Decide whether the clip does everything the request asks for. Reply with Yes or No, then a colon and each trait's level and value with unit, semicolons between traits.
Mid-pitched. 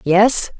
No: high, 205 Hz